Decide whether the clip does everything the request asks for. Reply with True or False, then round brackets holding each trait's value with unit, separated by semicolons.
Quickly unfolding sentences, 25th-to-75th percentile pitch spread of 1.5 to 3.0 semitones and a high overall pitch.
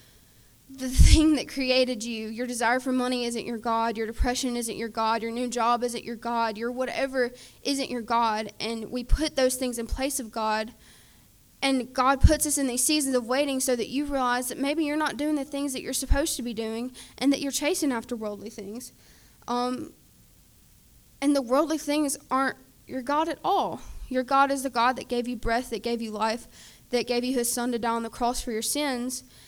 True (215 wpm; 2.7 semitones; 250 Hz)